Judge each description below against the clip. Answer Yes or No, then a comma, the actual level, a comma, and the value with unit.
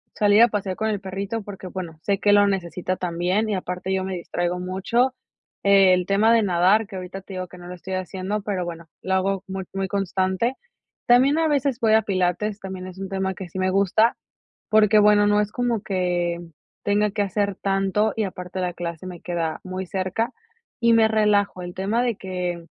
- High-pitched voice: Yes, high, 195 Hz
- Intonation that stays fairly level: Yes, narrow, 2.3 semitones